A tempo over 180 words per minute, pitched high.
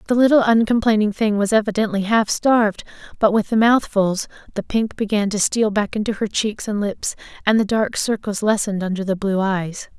Yes: average, 190 wpm; high, 210 Hz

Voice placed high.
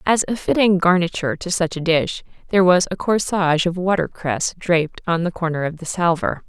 No: medium, 175 Hz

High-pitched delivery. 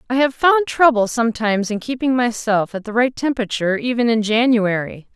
Yes: high, 235 Hz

